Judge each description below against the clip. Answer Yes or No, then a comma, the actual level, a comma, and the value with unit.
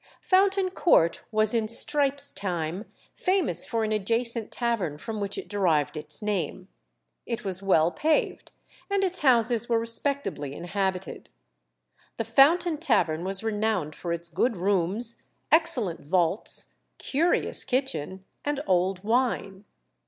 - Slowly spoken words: Yes, slow, 130 wpm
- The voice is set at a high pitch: Yes, high, 215 Hz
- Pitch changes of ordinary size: No, wide, 6.3 semitones